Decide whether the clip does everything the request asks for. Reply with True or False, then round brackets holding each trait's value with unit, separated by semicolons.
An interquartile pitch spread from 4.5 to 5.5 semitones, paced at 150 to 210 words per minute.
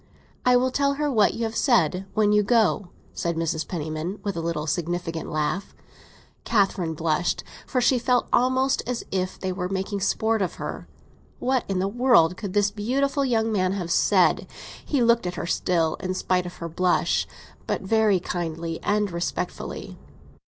True (5.0 semitones; 165 wpm)